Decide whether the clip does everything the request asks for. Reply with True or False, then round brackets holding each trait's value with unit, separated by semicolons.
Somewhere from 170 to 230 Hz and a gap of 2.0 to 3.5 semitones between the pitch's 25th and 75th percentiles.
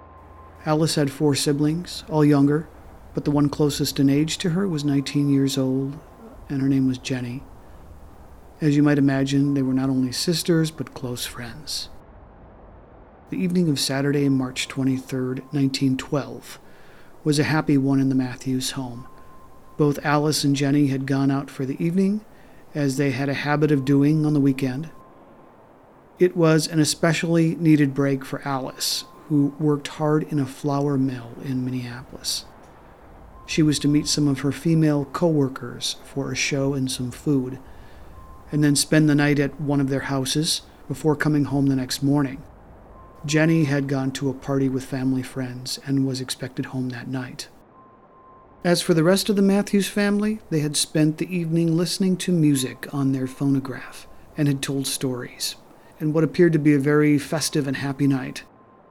False (140 Hz; 2.4 semitones)